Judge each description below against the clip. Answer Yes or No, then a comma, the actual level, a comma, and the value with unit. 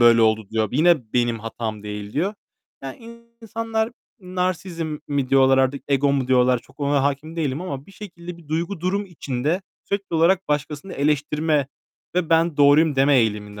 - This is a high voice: No, medium, 145 Hz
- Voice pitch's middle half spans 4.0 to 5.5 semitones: Yes, average, 5.1 semitones